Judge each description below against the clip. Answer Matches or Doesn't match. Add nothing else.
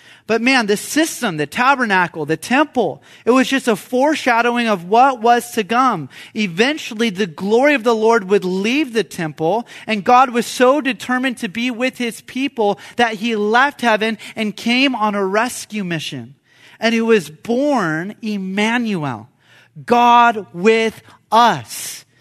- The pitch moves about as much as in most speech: Matches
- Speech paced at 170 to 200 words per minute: Doesn't match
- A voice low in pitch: Doesn't match